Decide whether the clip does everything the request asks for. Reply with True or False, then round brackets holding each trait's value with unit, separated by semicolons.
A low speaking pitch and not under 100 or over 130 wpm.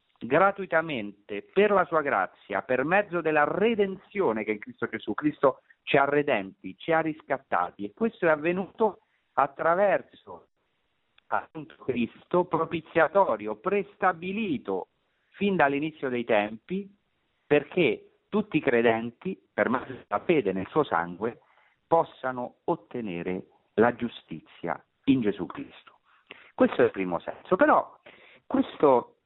False (150 Hz; 120 wpm)